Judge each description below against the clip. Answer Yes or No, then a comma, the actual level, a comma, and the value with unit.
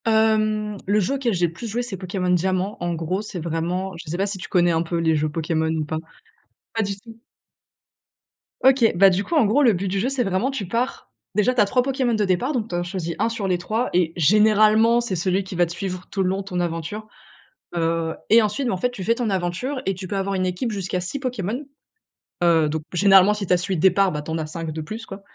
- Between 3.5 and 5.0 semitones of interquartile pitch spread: Yes, average, 3.9 semitones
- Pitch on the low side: No, high, 195 Hz